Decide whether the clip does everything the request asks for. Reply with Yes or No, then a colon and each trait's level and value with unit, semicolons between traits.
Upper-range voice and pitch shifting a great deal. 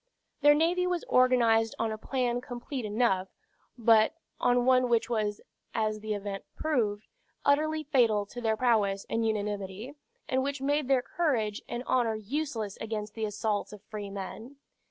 No: high, 230 Hz; average, 3.6 semitones